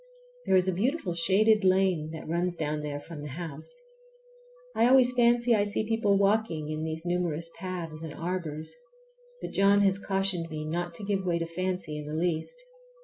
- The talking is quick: No, average, 185 wpm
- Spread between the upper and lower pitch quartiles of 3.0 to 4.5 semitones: Yes, average, 3.9 semitones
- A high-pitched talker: No, medium, 180 Hz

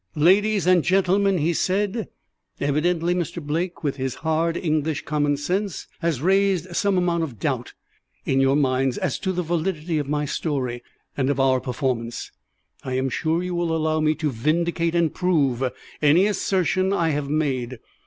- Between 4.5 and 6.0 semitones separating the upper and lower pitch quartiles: No, average, 4.0 semitones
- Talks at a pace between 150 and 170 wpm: Yes, average, 165 wpm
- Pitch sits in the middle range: Yes, medium, 160 Hz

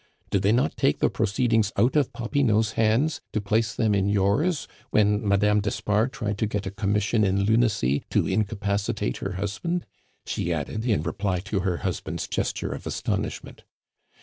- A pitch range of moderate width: No, narrow, 2.3 semitones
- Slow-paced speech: No, average, 165 wpm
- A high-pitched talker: No, low, 105 Hz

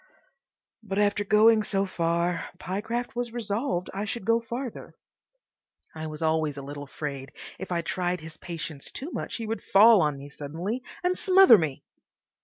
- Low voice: No, high, 190 Hz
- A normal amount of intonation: No, wide, 6.2 semitones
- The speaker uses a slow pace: No, average, 165 wpm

